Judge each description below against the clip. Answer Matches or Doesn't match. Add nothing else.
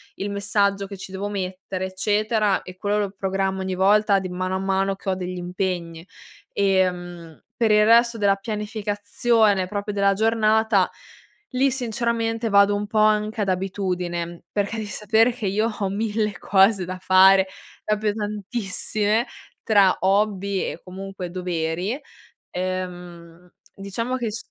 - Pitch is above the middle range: Matches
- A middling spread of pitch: Doesn't match